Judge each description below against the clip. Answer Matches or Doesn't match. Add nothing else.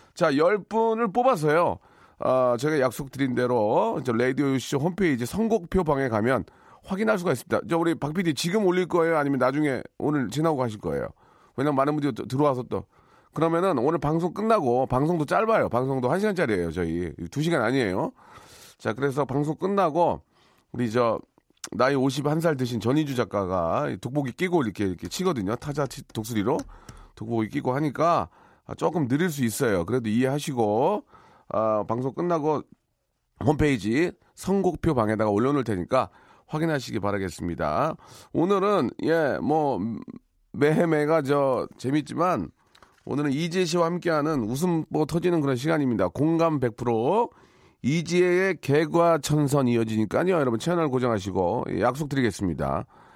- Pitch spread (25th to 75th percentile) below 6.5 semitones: Matches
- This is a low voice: Doesn't match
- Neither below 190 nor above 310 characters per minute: Doesn't match